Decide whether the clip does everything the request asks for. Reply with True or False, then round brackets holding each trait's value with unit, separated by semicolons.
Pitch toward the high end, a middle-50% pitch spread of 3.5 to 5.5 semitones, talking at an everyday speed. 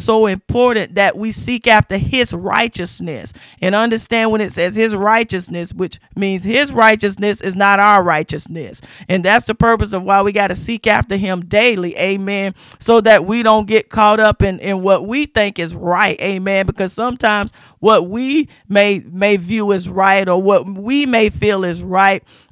False (200 Hz; 2.7 semitones; 180 wpm)